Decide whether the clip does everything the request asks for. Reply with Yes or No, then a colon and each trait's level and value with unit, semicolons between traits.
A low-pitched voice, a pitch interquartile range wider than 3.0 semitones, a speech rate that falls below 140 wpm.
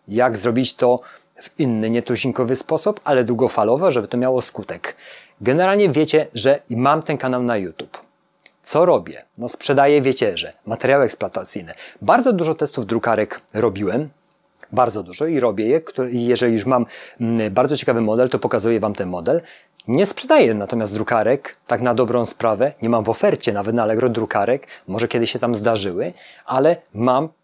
No: low, 125 Hz; average, 3.5 semitones; fast, 160 wpm